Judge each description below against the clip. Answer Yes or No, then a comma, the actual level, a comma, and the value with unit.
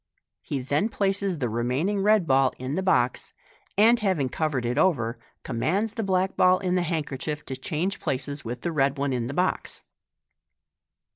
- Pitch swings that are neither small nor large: No, wide, 6.4 semitones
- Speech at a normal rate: Yes, average, 170 wpm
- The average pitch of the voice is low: No, medium, 155 Hz